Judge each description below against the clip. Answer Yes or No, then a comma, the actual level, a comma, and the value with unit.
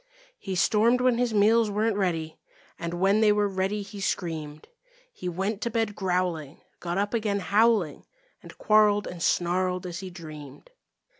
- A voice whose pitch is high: Yes, high, 195 Hz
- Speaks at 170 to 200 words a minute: No, average, 160 wpm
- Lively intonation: No, average, 3.4 semitones